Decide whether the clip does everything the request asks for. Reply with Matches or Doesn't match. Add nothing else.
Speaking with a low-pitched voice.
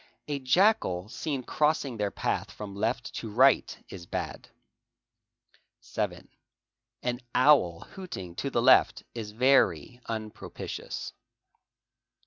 Matches